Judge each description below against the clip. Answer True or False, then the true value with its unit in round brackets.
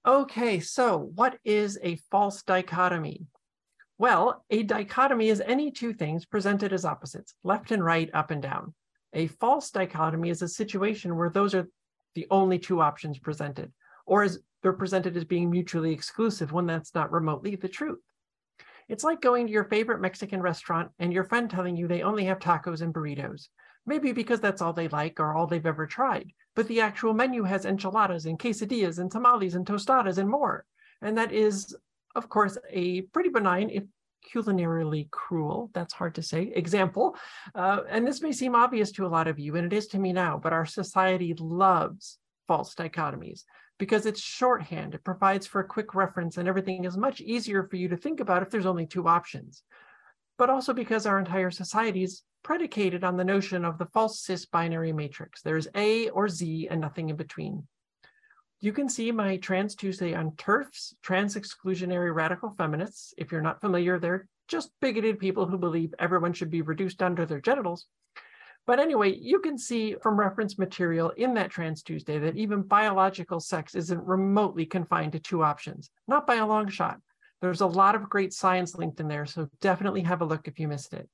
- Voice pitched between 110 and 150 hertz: False (190 Hz)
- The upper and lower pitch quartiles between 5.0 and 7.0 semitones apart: False (4.2 semitones)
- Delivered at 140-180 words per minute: False (190 wpm)